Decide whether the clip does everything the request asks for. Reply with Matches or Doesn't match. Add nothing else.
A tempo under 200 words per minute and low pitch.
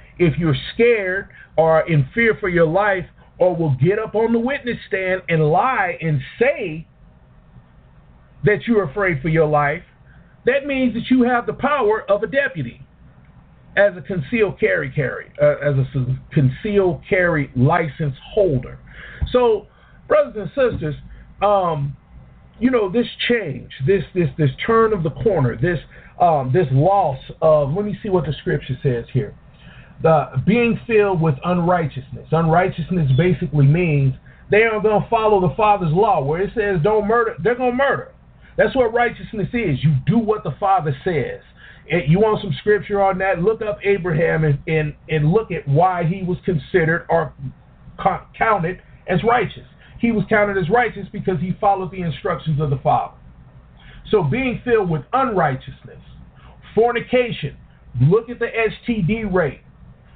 Doesn't match